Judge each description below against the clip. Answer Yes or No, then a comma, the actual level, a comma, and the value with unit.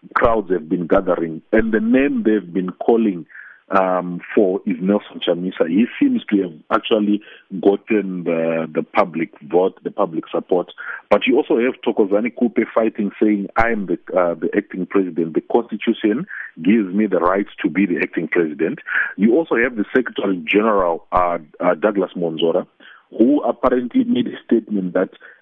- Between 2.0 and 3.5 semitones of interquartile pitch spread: No, average, 4.1 semitones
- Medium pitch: No, low, 105 Hz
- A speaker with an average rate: Yes, average, 165 wpm